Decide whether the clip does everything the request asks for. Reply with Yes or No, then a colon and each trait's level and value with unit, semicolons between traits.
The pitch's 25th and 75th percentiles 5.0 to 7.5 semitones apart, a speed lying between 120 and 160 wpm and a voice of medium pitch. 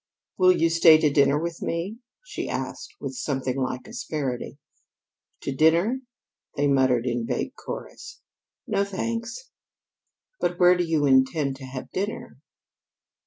Yes: wide, 5.5 semitones; slow, 135 wpm; medium, 160 Hz